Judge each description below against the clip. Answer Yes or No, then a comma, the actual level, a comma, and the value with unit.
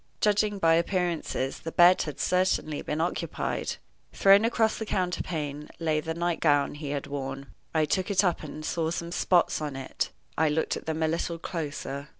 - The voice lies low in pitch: No, medium, 165 Hz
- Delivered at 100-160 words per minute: No, average, 175 wpm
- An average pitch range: Yes, average, 3.2 semitones